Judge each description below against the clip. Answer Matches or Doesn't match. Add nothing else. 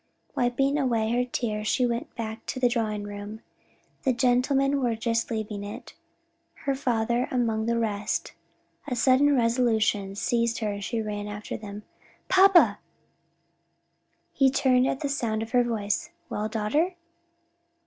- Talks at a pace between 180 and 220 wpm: Doesn't match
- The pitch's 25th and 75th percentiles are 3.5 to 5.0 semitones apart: Doesn't match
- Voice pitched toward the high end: Matches